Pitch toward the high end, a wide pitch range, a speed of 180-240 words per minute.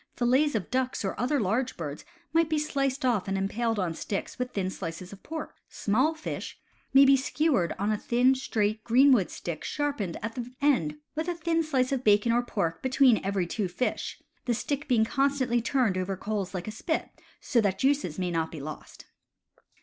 Yes: high, 235 Hz; wide, 5.9 semitones; average, 195 wpm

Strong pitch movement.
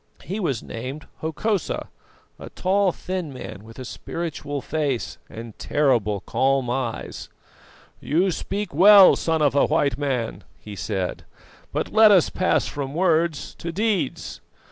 Yes: wide, 6.1 semitones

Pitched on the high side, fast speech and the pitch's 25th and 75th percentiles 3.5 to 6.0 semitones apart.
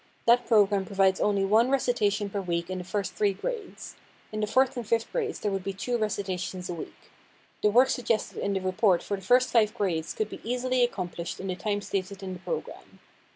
Yes: high, 205 Hz; fast, 215 wpm; average, 3.8 semitones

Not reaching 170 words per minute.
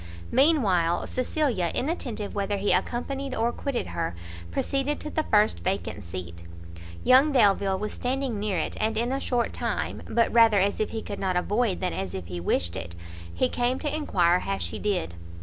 No: average, 185 wpm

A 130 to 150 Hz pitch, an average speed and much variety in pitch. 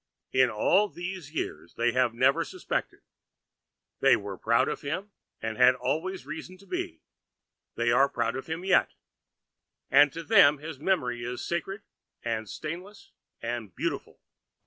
Yes: medium, 140 Hz; average, 145 wpm; wide, 7.4 semitones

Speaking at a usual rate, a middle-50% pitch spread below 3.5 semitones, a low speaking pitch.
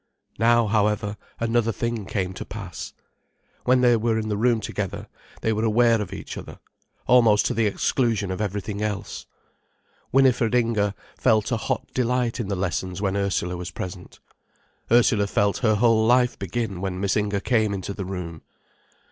Yes: average, 165 wpm; average, 2.9 semitones; low, 105 Hz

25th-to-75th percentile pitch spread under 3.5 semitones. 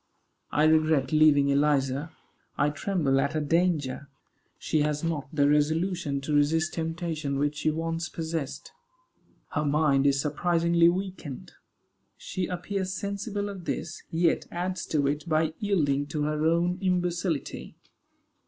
Yes: average, 2.9 semitones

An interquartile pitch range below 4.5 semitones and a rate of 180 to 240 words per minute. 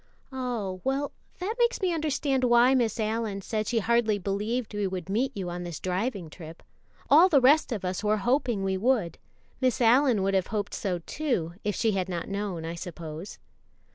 No: average, 5.3 semitones; average, 190 wpm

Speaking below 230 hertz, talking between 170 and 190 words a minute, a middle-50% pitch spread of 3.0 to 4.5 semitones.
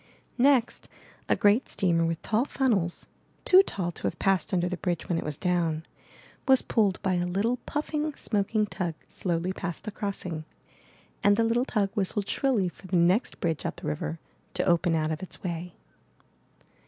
Yes: high, 190 Hz; average, 175 wpm; average, 4.1 semitones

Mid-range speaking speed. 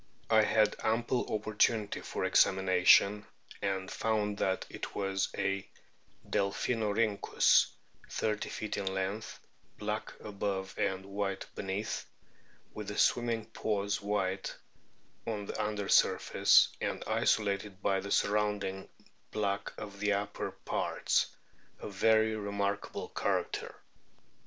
No: slow, 115 wpm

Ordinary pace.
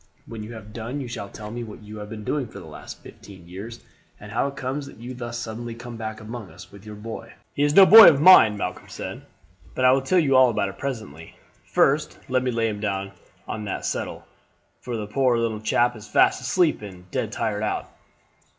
No: fast, 230 wpm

